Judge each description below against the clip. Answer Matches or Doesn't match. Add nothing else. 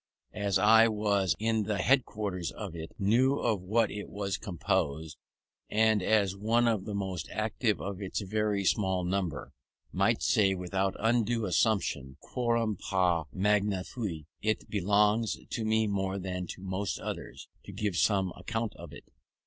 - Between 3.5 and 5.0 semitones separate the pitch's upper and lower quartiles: Doesn't match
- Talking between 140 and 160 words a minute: Matches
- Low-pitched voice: Matches